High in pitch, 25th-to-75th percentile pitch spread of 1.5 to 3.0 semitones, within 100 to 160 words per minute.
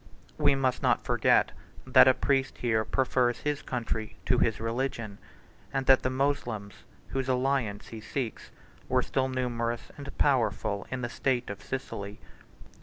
No: low, 125 Hz; average, 2.7 semitones; average, 155 wpm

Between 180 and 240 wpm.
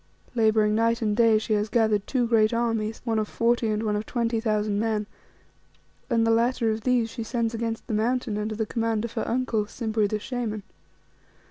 Yes: average, 200 wpm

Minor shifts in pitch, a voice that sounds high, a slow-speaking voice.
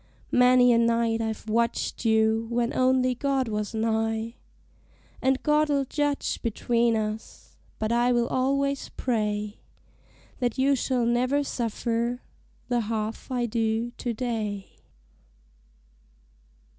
Yes: narrow, 2.3 semitones; high, 235 Hz; slow, 115 wpm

